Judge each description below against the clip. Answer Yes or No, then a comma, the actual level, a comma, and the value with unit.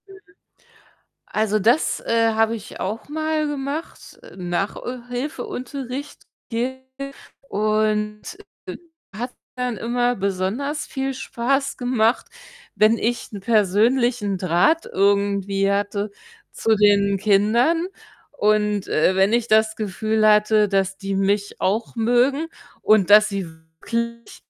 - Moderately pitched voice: No, high, 220 Hz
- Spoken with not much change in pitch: No, average, 3.5 semitones